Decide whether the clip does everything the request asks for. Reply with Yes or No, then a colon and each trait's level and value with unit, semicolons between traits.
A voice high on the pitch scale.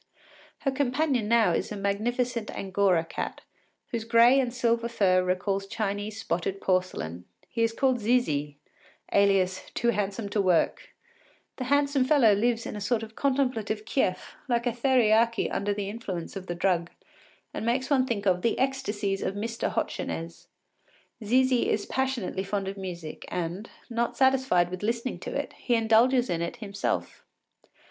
Yes: high, 220 Hz